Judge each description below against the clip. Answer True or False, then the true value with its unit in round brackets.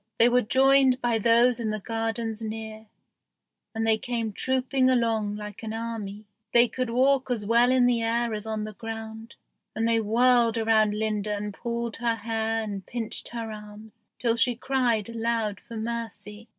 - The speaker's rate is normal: True (175 wpm)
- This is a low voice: False (225 Hz)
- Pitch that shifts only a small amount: True (1.6 semitones)